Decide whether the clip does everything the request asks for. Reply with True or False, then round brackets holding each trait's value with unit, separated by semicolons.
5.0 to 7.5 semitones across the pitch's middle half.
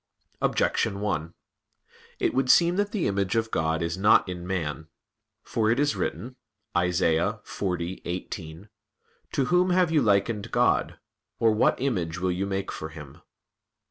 True (5.4 semitones)